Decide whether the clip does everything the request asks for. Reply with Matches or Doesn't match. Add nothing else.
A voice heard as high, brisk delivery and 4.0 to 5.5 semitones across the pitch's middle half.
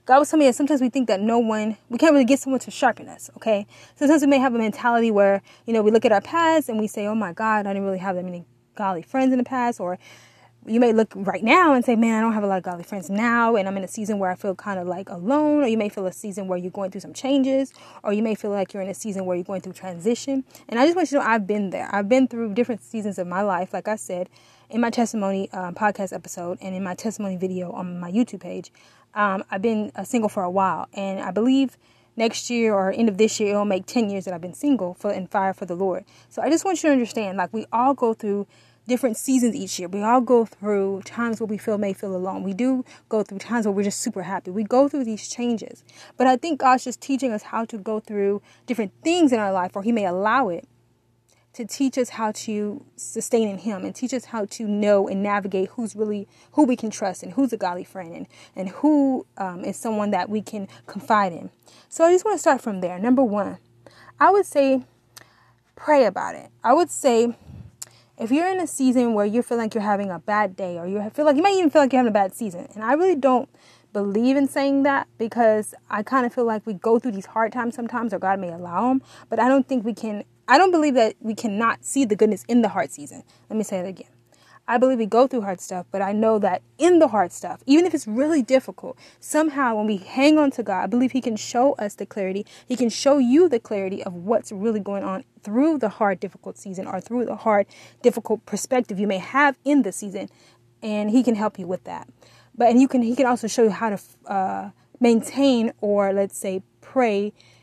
Matches